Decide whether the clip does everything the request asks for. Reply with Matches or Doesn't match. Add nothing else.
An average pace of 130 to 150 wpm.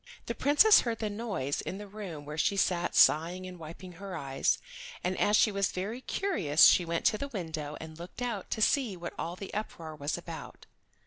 Doesn't match